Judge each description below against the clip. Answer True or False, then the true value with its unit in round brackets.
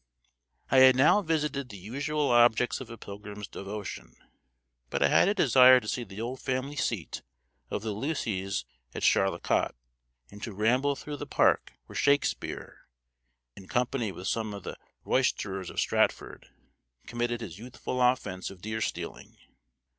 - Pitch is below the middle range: True (120 Hz)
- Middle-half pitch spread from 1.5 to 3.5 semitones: False (4.3 semitones)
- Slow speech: False (155 wpm)